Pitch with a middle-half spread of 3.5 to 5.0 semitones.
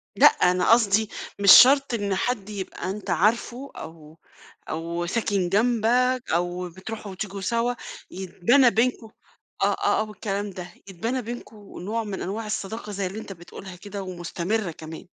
Yes: average, 3.9 semitones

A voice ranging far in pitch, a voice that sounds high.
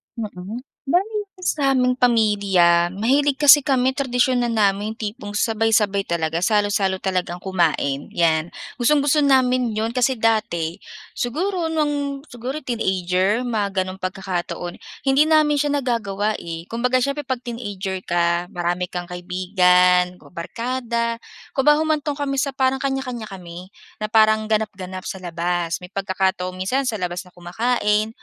Yes: wide, 5.9 semitones; high, 215 Hz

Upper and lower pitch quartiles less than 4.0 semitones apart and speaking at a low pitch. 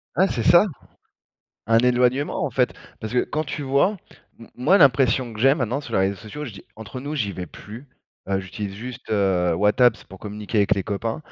No: average, 4.7 semitones; low, 120 Hz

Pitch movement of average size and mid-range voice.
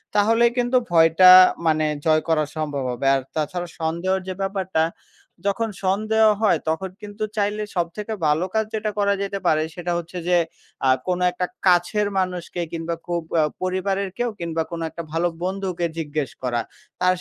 Yes: average, 3.5 semitones; medium, 180 Hz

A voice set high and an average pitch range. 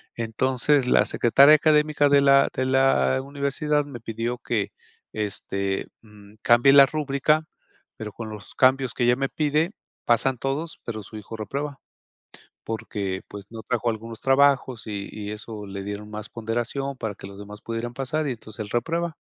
No: low, 120 Hz; average, 4.4 semitones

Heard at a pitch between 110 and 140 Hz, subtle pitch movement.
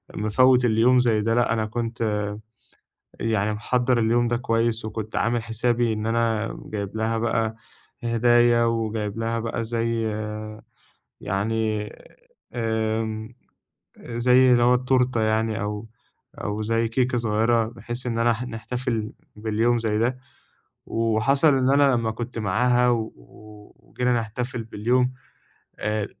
Yes: low, 115 Hz; narrow, 1.6 semitones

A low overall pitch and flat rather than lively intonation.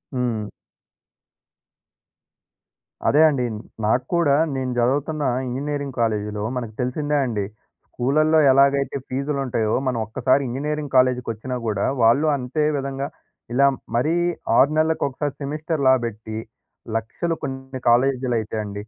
No: low, 130 Hz; average, 3.3 semitones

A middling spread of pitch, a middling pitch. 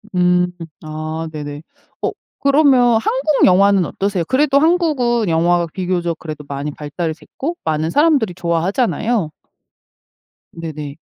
No: wide, 7.5 semitones; medium, 180 Hz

